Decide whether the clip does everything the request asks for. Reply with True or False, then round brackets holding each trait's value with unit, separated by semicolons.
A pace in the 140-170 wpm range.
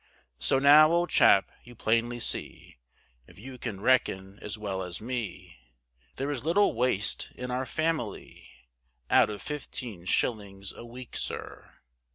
True (145 wpm)